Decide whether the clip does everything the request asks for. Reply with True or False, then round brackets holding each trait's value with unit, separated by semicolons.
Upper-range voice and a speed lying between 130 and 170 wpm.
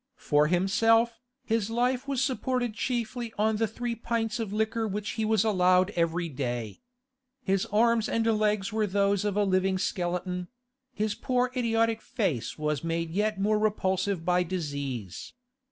True (210 Hz; 155 wpm)